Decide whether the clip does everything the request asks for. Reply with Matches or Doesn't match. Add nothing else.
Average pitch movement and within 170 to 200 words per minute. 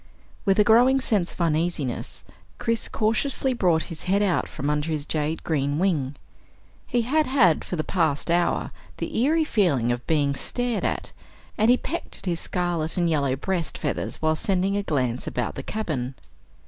Doesn't match